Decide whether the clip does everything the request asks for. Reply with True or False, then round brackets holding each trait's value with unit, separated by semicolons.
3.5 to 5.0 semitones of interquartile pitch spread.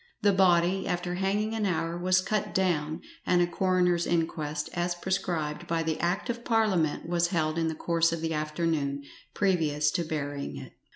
False (2.9 semitones)